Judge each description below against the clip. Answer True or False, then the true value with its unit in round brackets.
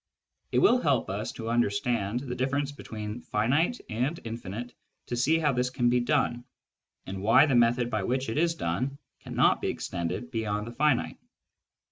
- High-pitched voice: False (120 Hz)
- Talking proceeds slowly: False (170 wpm)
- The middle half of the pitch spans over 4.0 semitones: False (3.5 semitones)